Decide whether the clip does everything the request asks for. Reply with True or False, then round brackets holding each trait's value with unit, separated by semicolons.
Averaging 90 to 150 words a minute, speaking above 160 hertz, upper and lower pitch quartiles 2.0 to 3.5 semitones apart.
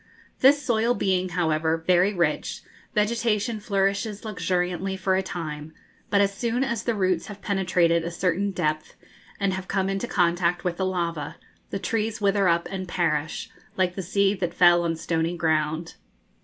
False (165 wpm; 185 Hz; 2.9 semitones)